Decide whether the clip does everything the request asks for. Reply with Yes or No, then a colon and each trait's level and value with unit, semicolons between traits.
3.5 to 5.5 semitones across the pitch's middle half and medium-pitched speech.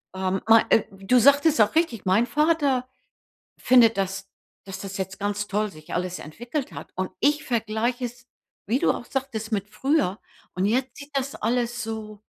No: average, 4.7 semitones; high, 225 Hz